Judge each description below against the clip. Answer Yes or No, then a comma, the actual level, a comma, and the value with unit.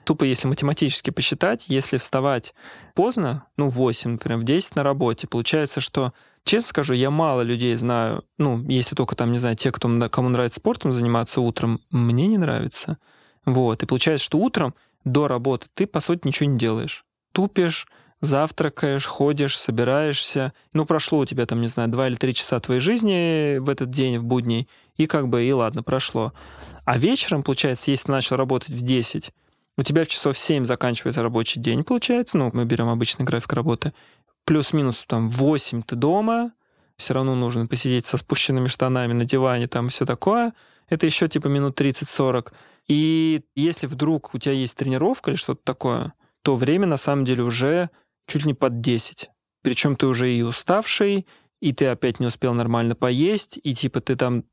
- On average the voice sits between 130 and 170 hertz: Yes, low, 135 Hz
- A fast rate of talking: Yes, fast, 180 wpm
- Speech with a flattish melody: No, average, 3.7 semitones